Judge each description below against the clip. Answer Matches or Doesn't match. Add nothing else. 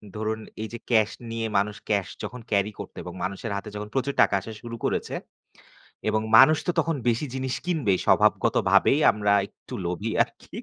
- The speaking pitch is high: Doesn't match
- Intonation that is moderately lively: Matches